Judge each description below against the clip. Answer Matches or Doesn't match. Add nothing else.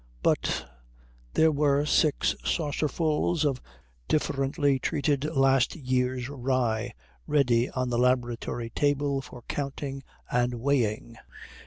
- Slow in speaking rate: Matches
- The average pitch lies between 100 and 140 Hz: Matches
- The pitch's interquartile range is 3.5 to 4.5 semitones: Doesn't match